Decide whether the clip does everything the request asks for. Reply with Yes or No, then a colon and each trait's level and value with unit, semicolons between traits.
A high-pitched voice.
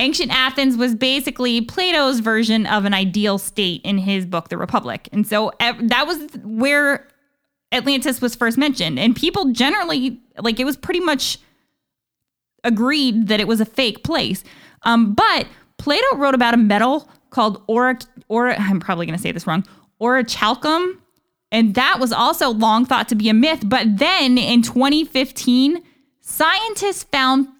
Yes: very high, 250 Hz